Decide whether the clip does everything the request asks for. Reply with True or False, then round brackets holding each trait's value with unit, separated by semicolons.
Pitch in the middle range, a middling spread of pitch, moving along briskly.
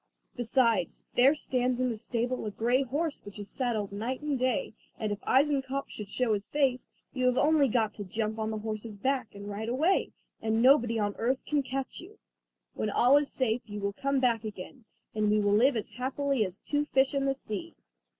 False (245 Hz; 4.0 semitones; 210 wpm)